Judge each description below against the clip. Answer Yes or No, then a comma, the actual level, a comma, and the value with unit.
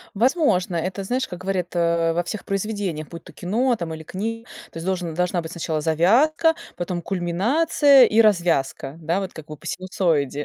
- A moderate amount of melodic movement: Yes, average, 4.3 semitones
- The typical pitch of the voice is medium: Yes, medium, 180 Hz